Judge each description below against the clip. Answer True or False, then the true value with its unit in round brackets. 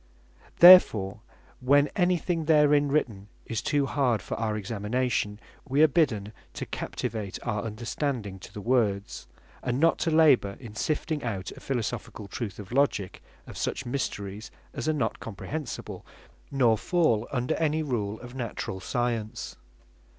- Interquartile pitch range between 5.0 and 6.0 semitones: True (5.6 semitones)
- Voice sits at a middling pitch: False (120 Hz)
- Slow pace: False (145 wpm)